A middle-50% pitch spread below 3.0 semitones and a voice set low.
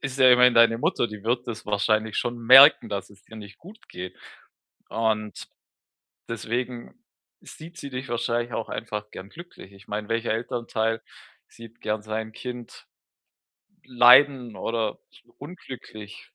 Yes: narrow, 2.6 semitones; low, 115 Hz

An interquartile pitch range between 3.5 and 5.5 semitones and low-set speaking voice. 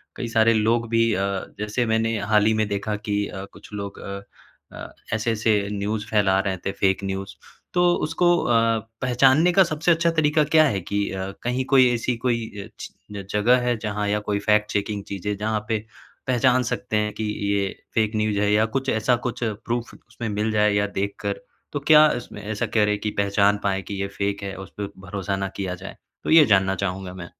No: average, 2.7 semitones; low, 105 Hz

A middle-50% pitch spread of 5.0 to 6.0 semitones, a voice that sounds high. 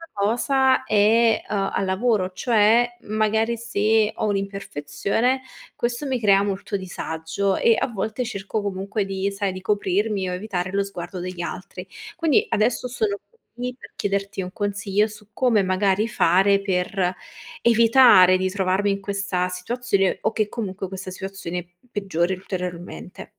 No: average, 2.8 semitones; high, 200 Hz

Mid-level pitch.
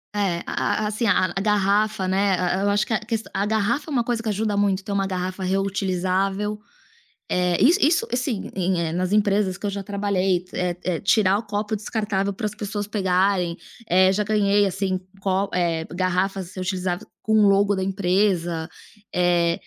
No: high, 195 Hz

